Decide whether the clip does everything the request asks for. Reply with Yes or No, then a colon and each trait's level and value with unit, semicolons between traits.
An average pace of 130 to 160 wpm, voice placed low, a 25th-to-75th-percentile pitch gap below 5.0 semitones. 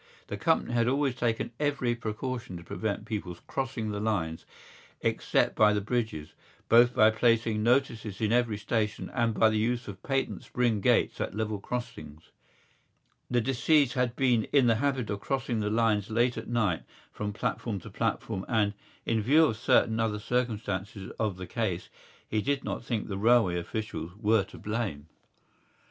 No: average, 170 wpm; low, 110 Hz; average, 2.8 semitones